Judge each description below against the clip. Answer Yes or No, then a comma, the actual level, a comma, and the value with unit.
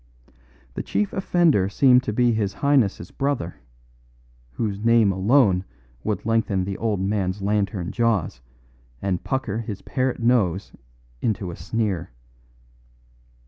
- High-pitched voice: No, low, 105 Hz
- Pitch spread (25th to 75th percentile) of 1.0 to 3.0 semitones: No, average, 3.8 semitones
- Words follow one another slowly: Yes, slow, 120 wpm